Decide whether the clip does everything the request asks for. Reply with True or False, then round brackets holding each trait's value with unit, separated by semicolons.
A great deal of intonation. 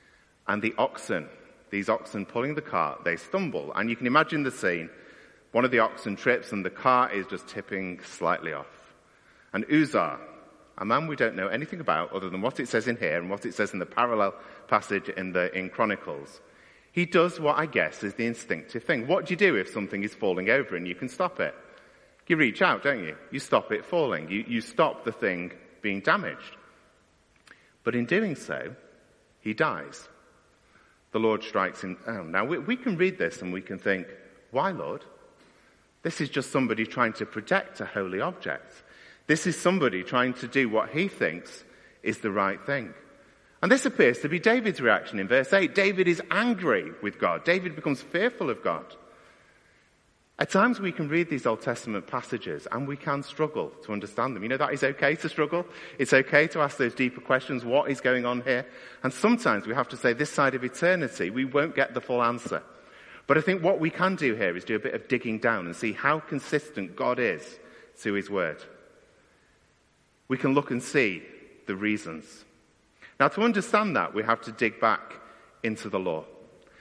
True (6.0 semitones)